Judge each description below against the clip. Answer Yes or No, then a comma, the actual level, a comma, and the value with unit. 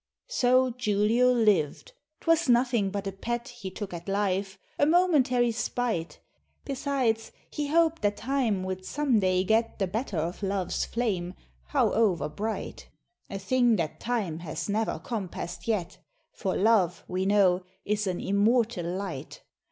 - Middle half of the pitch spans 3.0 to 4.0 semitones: No, average, 4.6 semitones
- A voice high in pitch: Yes, high, 210 Hz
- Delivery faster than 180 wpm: No, average, 145 wpm